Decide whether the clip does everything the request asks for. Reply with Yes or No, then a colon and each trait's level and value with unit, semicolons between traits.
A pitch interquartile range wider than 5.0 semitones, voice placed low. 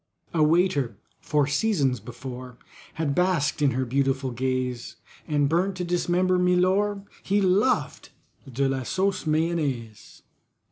No: wide, 5.6 semitones; medium, 150 Hz